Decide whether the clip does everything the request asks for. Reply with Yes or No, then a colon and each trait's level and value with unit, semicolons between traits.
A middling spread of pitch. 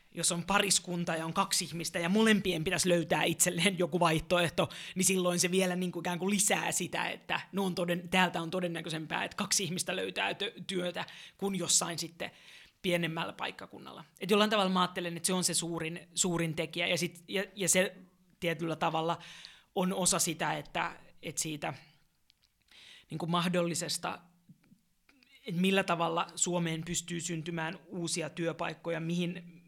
No: narrow, 1.7 semitones